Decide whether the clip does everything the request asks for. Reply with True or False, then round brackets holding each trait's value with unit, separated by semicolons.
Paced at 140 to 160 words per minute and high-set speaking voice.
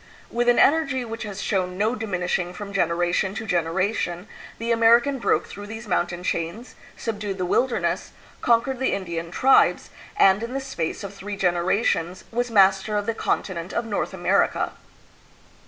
True (155 wpm; 205 Hz)